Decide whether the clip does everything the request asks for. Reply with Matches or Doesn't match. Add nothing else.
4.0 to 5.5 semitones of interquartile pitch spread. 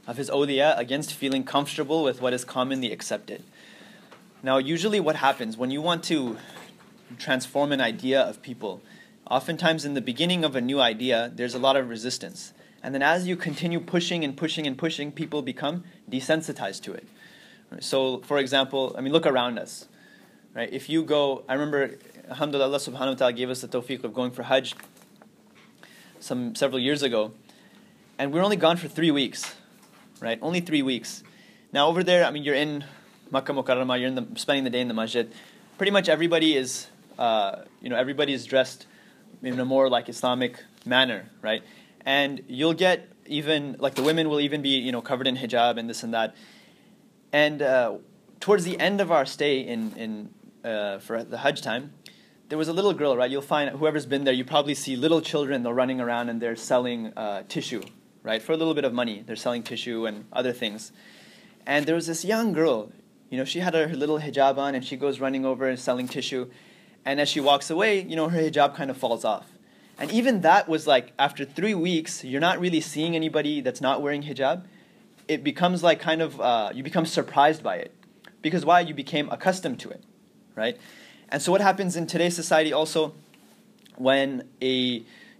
Matches